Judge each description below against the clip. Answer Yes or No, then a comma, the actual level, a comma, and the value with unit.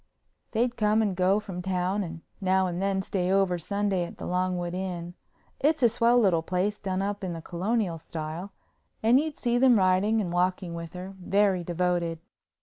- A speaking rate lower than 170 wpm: No, average, 175 wpm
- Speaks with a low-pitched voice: No, medium, 185 Hz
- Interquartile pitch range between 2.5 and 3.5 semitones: Yes, average, 2.8 semitones